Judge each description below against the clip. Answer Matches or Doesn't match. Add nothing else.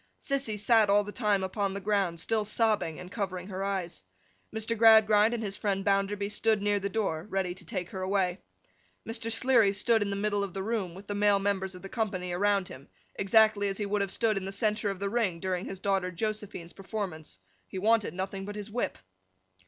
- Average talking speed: Doesn't match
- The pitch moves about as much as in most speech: Doesn't match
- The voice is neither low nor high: Doesn't match